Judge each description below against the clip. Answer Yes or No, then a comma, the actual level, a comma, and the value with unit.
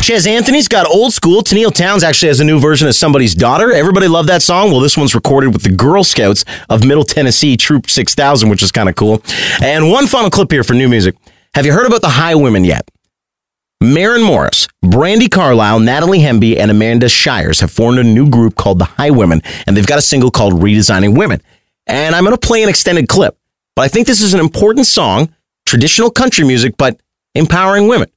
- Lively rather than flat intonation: Yes, wide, 8.6 semitones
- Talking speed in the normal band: No, fast, 215 wpm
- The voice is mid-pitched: Yes, medium, 145 Hz